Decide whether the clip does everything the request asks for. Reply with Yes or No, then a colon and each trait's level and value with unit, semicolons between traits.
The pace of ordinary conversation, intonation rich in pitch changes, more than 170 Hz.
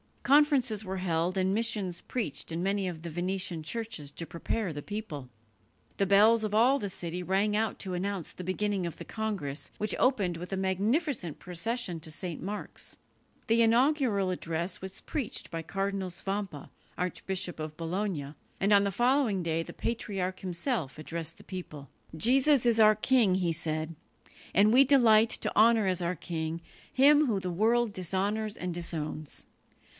No: average, 165 wpm; average, 4.3 semitones; high, 190 Hz